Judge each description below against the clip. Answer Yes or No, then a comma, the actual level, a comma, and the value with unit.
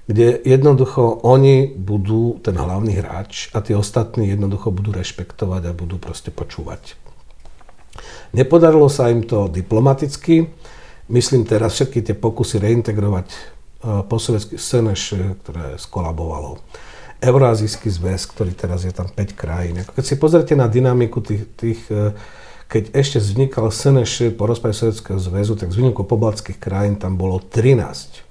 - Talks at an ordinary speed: Yes, average, 140 wpm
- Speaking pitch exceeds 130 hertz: No, low, 110 Hz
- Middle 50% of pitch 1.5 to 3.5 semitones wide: No, average, 4.4 semitones